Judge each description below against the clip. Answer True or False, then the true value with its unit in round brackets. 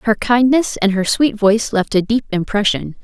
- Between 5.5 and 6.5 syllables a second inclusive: False (5.0 syllables/s)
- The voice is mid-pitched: False (215 Hz)